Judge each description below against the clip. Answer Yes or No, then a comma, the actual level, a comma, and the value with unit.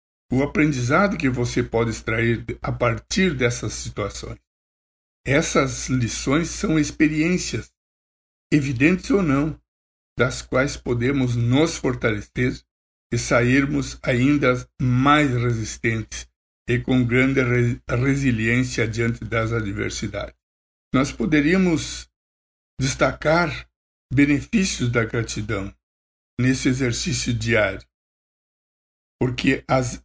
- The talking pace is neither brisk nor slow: No, slow, 90 wpm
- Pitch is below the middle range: Yes, low, 120 Hz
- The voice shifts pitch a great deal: Yes, wide, 7.0 semitones